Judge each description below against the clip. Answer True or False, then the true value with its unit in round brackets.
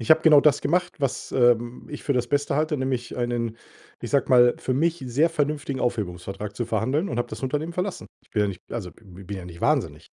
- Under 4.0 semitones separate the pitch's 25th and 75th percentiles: False (4.6 semitones)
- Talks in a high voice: False (125 Hz)